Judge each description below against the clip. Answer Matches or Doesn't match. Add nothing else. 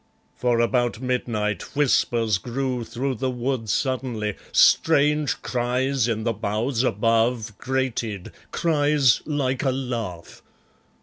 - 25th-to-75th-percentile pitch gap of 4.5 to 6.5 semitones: Doesn't match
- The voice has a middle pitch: Doesn't match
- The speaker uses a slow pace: Matches